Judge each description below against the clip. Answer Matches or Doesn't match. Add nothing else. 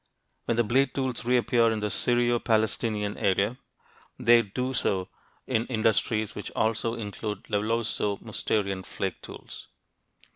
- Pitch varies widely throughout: Doesn't match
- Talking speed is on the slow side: Matches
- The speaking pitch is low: Matches